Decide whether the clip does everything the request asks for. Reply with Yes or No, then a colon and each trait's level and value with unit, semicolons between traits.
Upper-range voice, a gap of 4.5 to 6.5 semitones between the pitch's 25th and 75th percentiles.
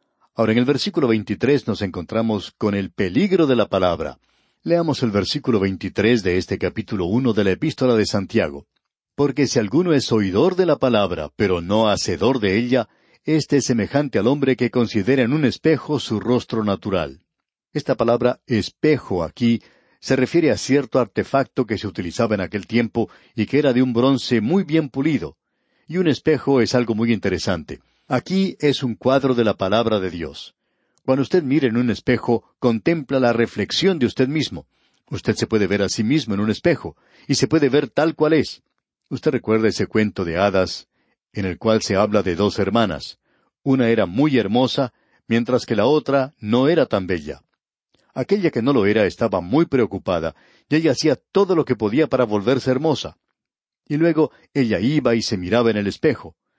No: low, 120 Hz; average, 4.8 semitones